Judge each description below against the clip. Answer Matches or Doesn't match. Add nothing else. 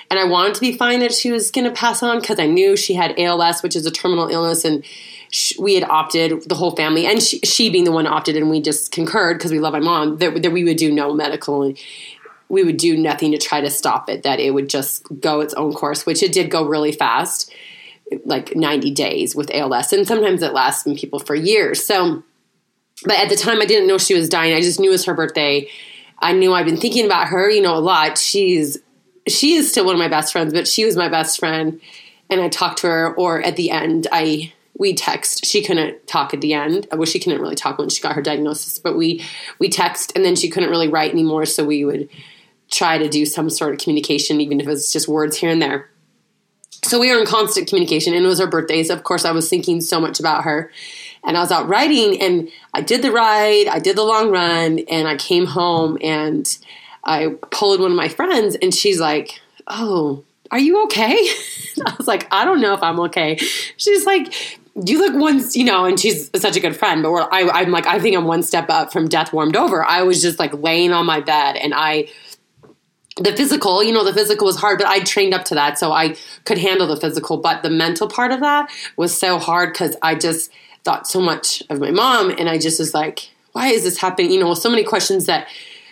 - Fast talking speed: Matches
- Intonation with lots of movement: Matches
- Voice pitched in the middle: Matches